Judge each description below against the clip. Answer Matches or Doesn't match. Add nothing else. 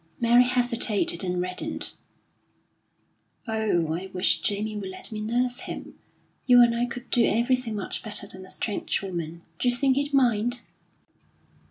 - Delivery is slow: Doesn't match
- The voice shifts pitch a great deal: Doesn't match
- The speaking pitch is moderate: Doesn't match